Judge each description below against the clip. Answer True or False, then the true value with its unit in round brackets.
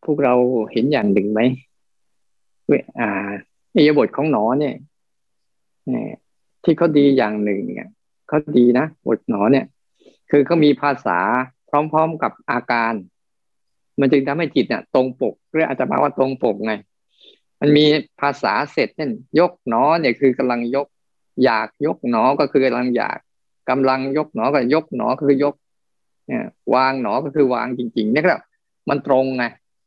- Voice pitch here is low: True (130 Hz)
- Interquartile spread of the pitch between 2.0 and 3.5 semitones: True (3.1 semitones)